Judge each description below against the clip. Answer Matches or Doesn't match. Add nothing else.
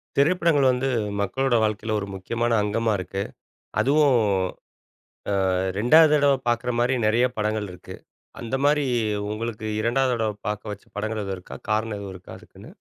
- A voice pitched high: Doesn't match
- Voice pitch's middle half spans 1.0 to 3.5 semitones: Doesn't match